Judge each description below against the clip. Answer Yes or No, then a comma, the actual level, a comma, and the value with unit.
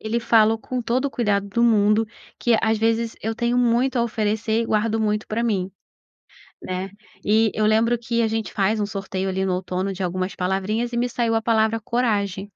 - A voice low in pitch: No, high, 220 Hz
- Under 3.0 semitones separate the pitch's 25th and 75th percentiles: Yes, narrow, 2.4 semitones